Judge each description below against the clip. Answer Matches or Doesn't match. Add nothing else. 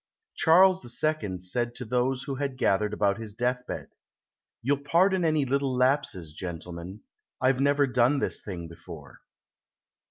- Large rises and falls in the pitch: Matches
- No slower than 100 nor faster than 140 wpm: Matches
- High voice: Doesn't match